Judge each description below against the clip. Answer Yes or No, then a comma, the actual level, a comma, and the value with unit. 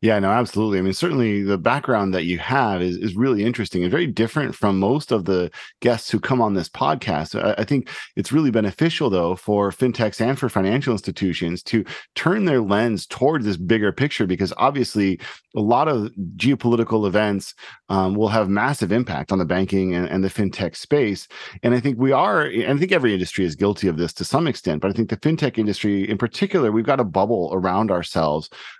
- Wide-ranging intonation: No, average, 4.0 semitones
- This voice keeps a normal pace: No, fast, 210 wpm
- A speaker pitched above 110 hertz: No, low, 105 Hz